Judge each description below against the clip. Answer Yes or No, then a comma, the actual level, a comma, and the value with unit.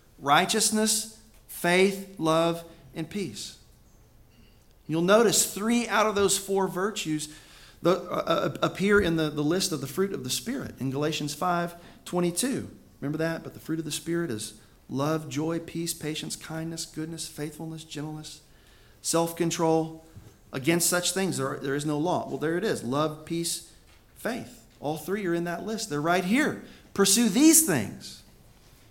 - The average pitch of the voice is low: No, medium, 165 Hz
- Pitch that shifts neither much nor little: Yes, average, 4.0 semitones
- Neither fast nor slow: Yes, average, 160 wpm